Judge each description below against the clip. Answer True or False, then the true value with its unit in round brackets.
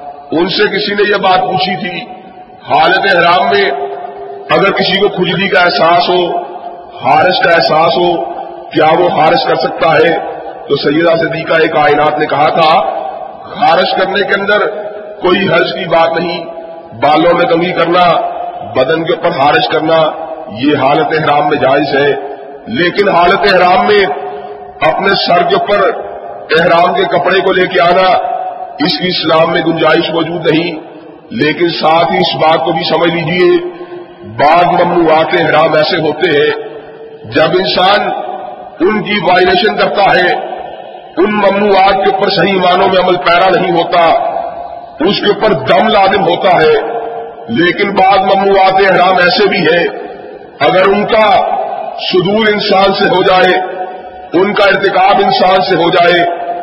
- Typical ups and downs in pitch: True (3.5 semitones)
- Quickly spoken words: False (155 wpm)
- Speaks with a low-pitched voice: False (185 Hz)